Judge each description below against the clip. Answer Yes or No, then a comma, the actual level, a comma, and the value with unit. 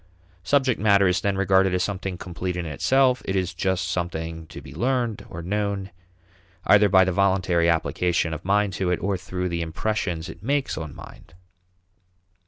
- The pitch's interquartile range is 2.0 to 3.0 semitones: Yes, average, 2.7 semitones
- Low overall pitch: Yes, very low, 95 Hz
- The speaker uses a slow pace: No, average, 175 wpm